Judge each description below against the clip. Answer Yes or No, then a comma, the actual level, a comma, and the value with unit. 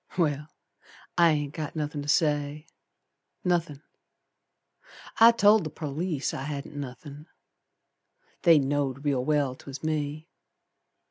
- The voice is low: No, medium, 150 Hz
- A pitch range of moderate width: No, narrow, 1.9 semitones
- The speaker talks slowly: Yes, slow, 115 wpm